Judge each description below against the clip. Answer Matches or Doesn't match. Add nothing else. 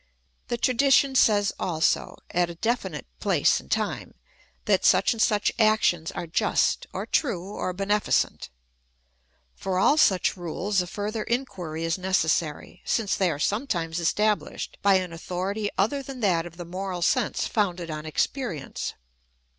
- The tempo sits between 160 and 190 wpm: Doesn't match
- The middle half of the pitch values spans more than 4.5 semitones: Doesn't match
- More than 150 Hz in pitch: Matches